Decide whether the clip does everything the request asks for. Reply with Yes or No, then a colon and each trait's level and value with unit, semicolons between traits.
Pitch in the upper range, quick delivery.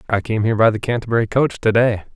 No: low, 110 Hz; fast, 225 wpm